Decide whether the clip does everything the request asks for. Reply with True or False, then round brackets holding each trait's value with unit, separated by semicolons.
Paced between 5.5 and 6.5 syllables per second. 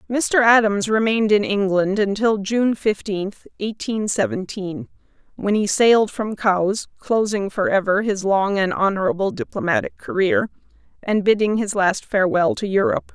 False (4.8 syllables/s)